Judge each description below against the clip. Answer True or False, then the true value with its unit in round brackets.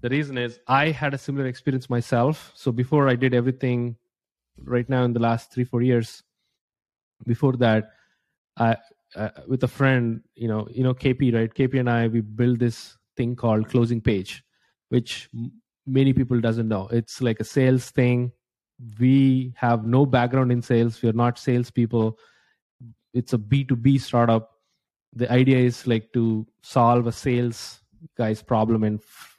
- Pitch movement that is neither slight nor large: False (2.0 semitones)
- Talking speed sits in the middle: True (165 wpm)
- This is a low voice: True (120 Hz)